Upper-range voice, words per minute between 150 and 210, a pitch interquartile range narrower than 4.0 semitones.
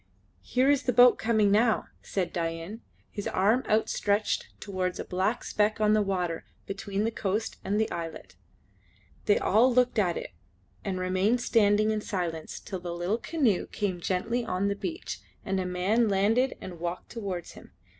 Yes: high, 205 Hz; average, 170 wpm; average, 3.5 semitones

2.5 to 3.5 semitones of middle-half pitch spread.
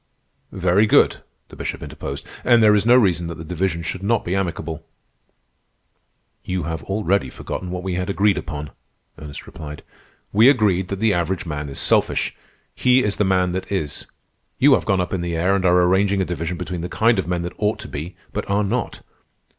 Yes: average, 2.9 semitones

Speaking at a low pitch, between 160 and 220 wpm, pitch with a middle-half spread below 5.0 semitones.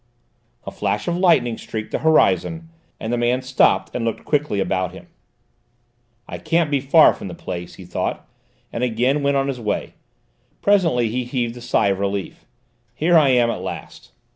No: low, 125 Hz; average, 180 wpm; average, 5.3 semitones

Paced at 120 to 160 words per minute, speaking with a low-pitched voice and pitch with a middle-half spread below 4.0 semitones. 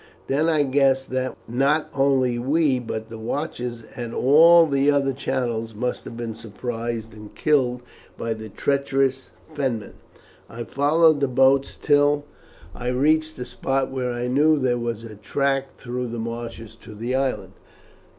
Yes: average, 155 wpm; low, 130 Hz; average, 2.9 semitones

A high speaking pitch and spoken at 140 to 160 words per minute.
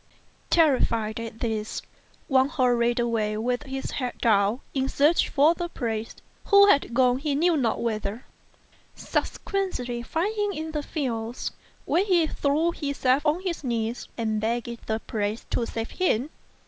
Yes: very high, 250 Hz; average, 150 wpm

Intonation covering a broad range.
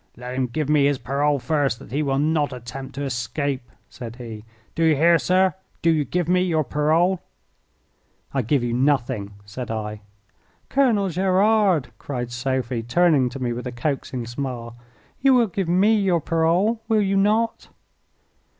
Yes: wide, 6.3 semitones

